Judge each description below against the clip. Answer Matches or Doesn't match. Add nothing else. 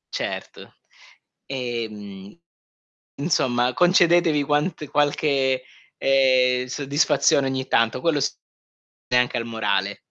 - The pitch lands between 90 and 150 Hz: Matches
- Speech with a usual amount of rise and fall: Matches